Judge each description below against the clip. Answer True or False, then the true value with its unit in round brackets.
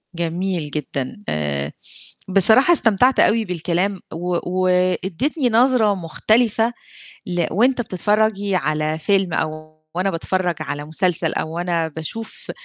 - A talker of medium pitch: True (180 Hz)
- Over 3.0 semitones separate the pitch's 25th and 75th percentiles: True (4.8 semitones)